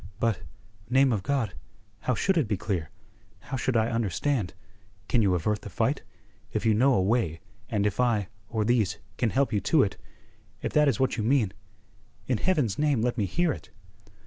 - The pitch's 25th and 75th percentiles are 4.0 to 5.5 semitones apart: Yes, average, 4.3 semitones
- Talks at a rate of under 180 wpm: No, average, 195 wpm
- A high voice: No, low, 115 Hz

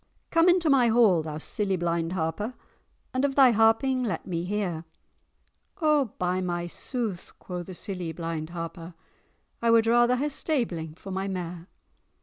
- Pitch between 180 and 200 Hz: Yes, high, 190 Hz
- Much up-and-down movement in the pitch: Yes, wide, 6.0 semitones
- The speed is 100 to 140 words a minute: No, average, 155 wpm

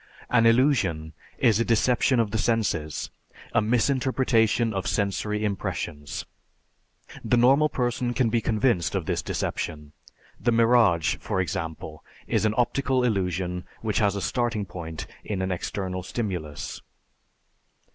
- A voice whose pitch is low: Yes, low, 110 Hz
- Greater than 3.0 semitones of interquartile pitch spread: Yes, average, 4.9 semitones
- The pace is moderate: No, slow, 130 wpm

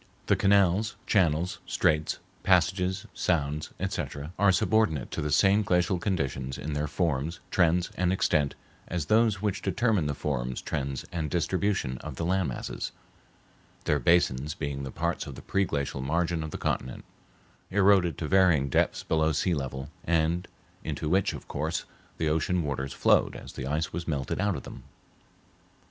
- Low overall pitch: Yes, very low, 80 Hz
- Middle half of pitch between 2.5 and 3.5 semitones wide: No, average, 4.2 semitones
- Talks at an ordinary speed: Yes, average, 160 wpm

